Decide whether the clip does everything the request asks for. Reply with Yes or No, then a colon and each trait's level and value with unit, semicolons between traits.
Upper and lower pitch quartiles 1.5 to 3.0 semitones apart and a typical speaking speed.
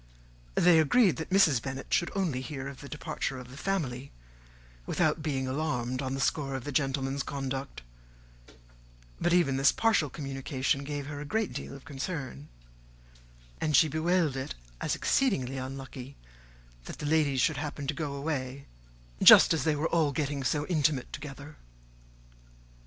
Yes: average, 2.7 semitones; average, 155 wpm